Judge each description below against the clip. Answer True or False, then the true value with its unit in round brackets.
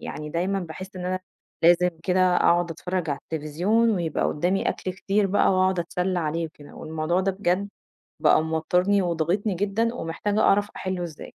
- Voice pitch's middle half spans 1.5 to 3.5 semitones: True (2.8 semitones)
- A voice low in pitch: False (180 Hz)